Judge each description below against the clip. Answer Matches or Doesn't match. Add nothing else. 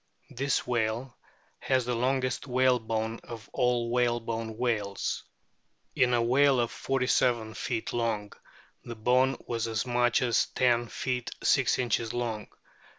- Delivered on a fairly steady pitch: Matches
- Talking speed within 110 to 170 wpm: Matches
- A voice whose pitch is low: Matches